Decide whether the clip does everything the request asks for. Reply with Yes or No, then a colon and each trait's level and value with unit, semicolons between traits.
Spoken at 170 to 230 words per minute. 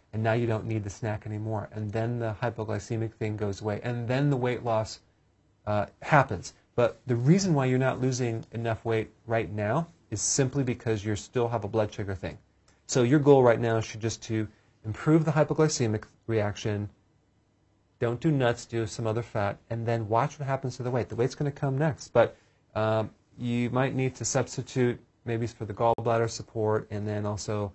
Yes: average, 195 wpm